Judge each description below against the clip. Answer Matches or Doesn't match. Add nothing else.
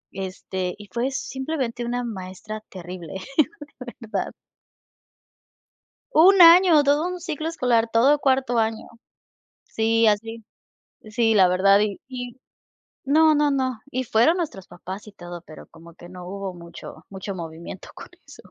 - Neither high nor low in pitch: Doesn't match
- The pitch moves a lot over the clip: Matches